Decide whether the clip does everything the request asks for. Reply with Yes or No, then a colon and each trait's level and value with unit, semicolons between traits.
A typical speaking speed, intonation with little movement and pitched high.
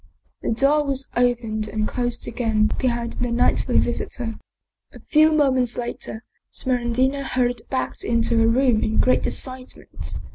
Yes: average, 145 wpm; narrow, 2.1 semitones; high, 245 Hz